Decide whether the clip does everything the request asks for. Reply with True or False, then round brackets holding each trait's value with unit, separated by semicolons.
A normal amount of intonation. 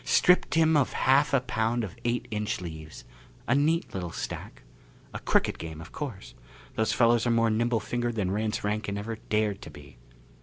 True (3.4 semitones)